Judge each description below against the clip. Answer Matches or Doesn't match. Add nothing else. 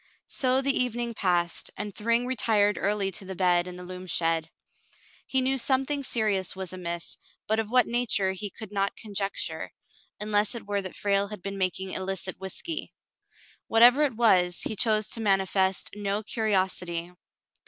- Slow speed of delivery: Doesn't match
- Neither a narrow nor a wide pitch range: Matches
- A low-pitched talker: Doesn't match